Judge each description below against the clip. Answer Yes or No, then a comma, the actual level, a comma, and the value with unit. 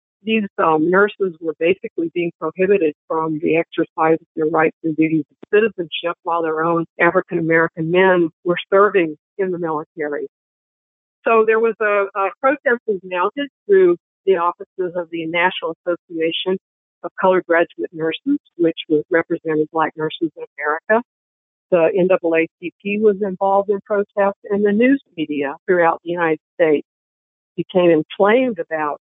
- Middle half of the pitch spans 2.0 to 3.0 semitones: No, average, 3.9 semitones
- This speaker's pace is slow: No, average, 145 wpm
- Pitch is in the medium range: Yes, medium, 175 Hz